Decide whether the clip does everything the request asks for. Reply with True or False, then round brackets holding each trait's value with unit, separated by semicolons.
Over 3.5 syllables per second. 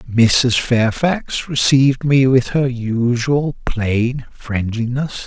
False (3.0 syllables/s)